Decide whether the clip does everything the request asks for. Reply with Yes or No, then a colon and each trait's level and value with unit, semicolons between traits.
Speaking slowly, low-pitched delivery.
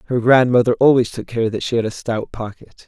No: fast, 230 wpm; low, 115 Hz